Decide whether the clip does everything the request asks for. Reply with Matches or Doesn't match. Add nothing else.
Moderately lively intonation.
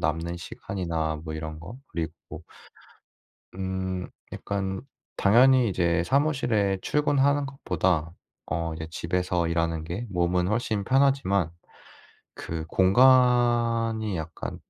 Doesn't match